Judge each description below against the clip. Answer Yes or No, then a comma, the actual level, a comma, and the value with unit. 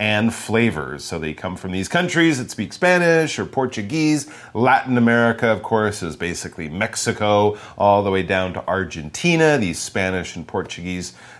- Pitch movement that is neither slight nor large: Yes, average, 4.9 semitones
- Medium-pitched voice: No, low, 105 Hz